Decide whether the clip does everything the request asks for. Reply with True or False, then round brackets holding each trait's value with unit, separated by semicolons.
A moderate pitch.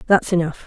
True (175 Hz)